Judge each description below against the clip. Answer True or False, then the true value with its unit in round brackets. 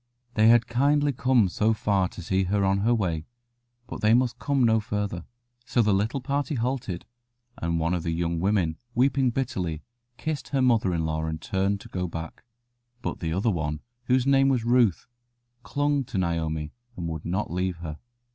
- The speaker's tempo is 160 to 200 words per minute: True (185 wpm)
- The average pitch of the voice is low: True (100 Hz)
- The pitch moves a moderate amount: False (6.6 semitones)